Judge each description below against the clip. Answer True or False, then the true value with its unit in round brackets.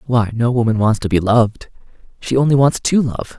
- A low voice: True (120 Hz)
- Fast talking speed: True (215 wpm)